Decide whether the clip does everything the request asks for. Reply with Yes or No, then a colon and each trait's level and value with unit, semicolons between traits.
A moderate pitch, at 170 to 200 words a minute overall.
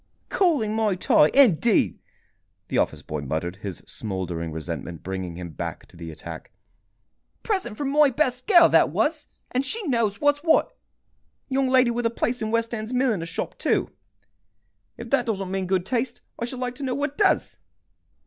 No: high, 230 Hz; average, 175 wpm